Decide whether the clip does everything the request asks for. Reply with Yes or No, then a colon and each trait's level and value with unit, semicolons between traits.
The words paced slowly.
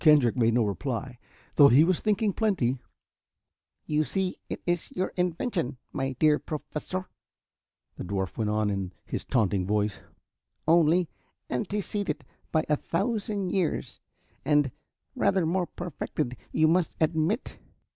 Yes: slow, 130 wpm